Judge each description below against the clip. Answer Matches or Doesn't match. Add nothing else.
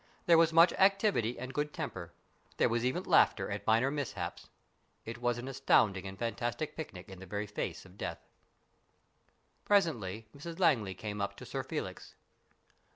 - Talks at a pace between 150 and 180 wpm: Matches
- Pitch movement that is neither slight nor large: Doesn't match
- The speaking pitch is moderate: Doesn't match